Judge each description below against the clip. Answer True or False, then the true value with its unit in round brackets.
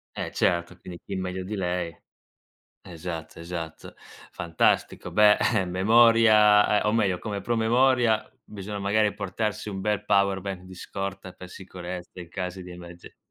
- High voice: False (95 Hz)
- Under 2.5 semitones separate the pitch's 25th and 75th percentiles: False (2.8 semitones)